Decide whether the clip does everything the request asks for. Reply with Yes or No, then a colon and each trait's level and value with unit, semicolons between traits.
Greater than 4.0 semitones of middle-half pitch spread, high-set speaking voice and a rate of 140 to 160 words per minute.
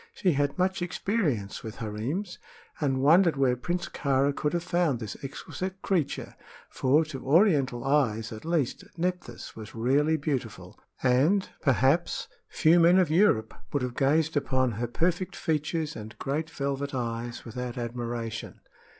No: wide, 5.5 semitones; medium, 140 Hz; average, 145 wpm